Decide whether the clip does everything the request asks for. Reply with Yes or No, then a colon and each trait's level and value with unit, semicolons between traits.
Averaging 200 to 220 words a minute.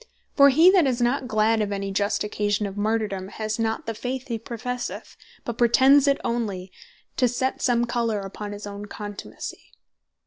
No: average, 175 wpm